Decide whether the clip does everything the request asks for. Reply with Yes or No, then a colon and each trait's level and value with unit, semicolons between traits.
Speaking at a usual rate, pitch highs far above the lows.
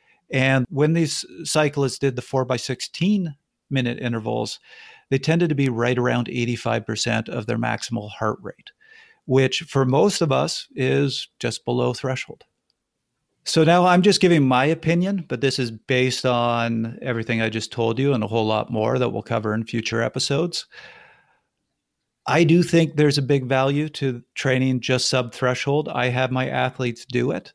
No: average, 170 wpm; average, 3.8 semitones